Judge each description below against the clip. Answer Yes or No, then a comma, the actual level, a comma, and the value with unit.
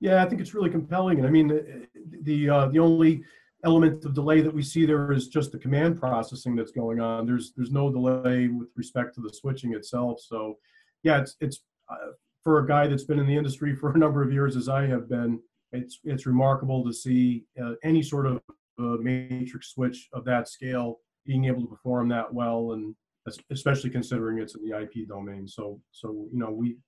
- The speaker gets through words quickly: Yes, fast, 210 wpm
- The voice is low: Yes, low, 130 Hz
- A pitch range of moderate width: Yes, average, 3.7 semitones